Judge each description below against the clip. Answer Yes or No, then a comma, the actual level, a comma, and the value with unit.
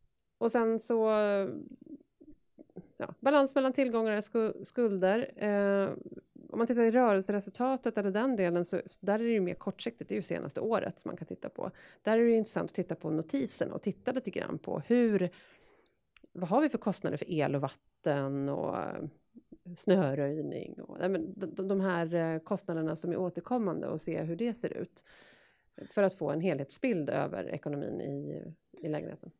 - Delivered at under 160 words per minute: No, average, 175 wpm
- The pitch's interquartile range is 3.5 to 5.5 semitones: Yes, average, 5.2 semitones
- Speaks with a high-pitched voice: Yes, high, 200 Hz